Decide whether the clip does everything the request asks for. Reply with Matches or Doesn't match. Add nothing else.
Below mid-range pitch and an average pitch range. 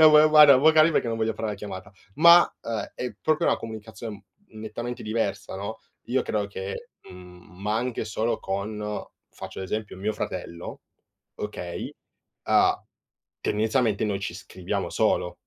Matches